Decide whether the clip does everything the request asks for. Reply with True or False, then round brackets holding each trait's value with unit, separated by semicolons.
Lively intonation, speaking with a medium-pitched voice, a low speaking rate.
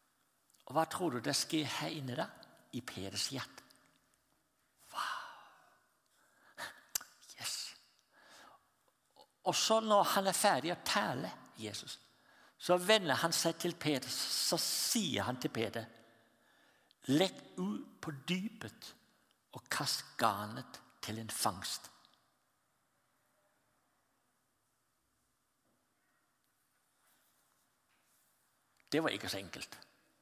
True (6.4 semitones; 160 Hz; 95 wpm)